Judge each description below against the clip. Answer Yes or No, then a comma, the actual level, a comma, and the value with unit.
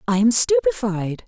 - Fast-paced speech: No, average, 140 wpm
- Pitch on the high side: Yes, high, 200 Hz